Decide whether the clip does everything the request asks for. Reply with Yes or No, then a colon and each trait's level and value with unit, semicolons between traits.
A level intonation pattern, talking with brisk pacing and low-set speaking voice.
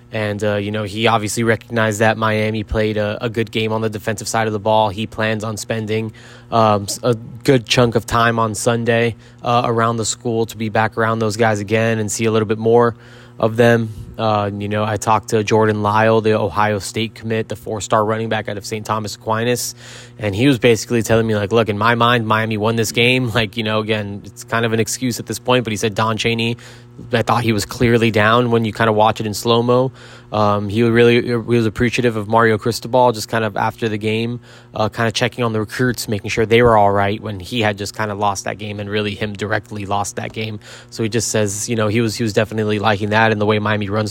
Yes: narrow, 1.6 semitones; fast, 250 wpm; low, 110 Hz